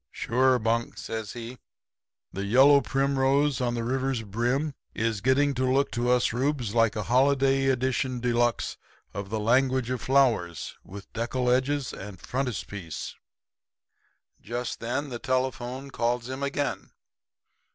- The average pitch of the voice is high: No, low, 125 Hz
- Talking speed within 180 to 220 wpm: No, average, 140 wpm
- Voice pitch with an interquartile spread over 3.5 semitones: No, narrow, 2.6 semitones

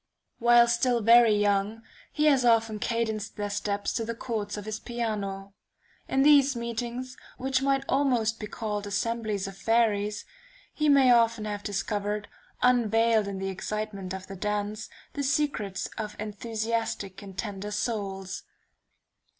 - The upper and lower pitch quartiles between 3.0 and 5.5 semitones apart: No, narrow, 2.6 semitones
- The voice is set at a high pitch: Yes, high, 220 Hz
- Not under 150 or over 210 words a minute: No, average, 140 wpm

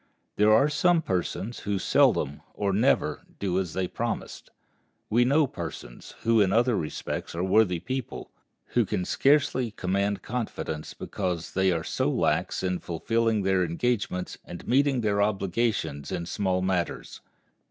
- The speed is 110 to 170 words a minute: Yes, average, 145 wpm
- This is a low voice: Yes, low, 100 Hz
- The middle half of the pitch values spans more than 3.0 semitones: Yes, average, 4.3 semitones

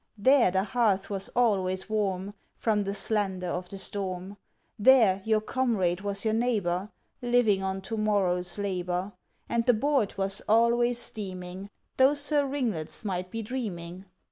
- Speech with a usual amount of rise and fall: Yes, average, 3.8 semitones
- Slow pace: No, average, 145 wpm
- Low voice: No, high, 205 Hz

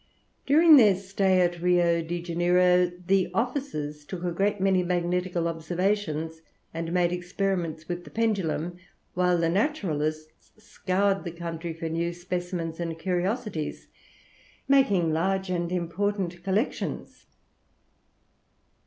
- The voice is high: No, medium, 180 Hz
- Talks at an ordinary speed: No, slow, 120 wpm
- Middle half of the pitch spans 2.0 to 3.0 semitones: Yes, narrow, 2.5 semitones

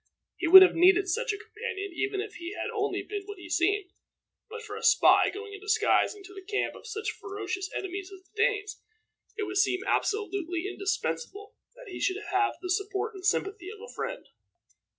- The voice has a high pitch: Yes, very high, 400 Hz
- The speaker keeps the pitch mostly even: Yes, narrow, 1.8 semitones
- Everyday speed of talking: Yes, average, 195 wpm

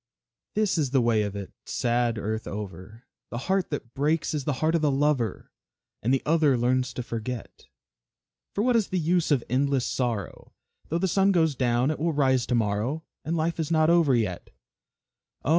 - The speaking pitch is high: No, low, 135 Hz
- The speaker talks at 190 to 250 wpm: Yes, average, 195 wpm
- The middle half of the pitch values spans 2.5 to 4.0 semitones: No, average, 5.3 semitones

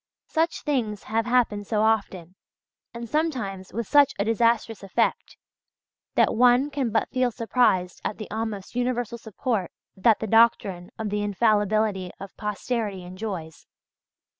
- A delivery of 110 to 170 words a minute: Yes, average, 140 wpm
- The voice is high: Yes, high, 220 Hz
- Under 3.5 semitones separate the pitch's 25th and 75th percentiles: Yes, average, 3.1 semitones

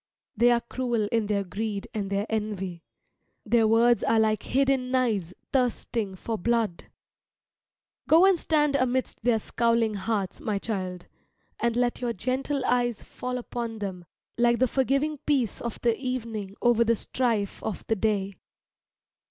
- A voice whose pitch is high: Yes, high, 230 Hz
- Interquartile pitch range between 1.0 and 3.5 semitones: Yes, average, 3.2 semitones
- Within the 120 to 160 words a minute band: Yes, average, 150 wpm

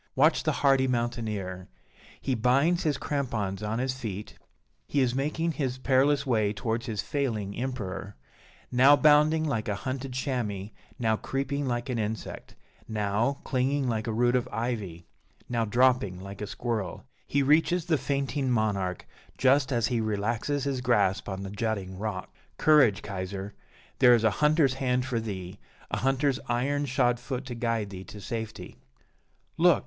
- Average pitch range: Yes, average, 4.3 semitones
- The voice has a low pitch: Yes, low, 120 Hz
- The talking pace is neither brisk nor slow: Yes, average, 160 wpm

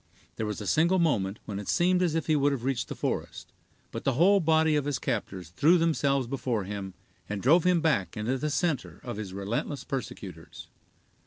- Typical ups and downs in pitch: No, wide, 7.1 semitones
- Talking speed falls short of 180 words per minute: No, average, 200 wpm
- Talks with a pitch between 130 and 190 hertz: Yes, low, 135 Hz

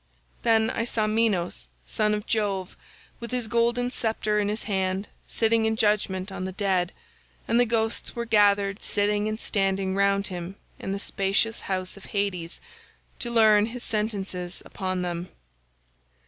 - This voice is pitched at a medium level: No, high, 205 Hz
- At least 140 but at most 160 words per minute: Yes, average, 155 wpm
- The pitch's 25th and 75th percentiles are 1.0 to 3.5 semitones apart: Yes, narrow, 2.6 semitones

